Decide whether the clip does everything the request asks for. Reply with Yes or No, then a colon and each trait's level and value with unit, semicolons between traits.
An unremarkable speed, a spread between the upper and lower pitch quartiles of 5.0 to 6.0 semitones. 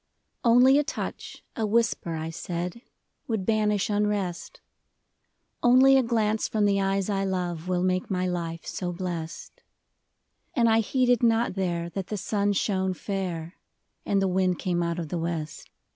No: average, 160 wpm; average, 3.8 semitones